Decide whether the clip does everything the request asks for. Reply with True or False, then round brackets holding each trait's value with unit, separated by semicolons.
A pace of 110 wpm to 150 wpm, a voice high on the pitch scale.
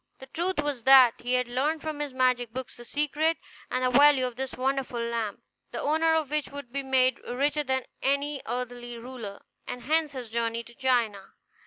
False (195 wpm; 260 Hz)